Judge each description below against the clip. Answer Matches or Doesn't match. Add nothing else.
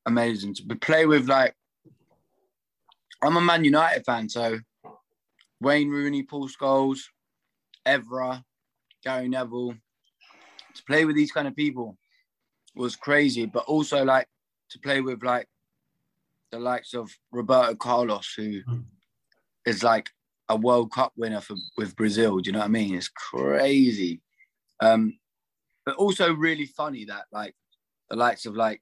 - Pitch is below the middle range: Matches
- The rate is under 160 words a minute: Matches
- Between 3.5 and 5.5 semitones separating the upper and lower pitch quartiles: Matches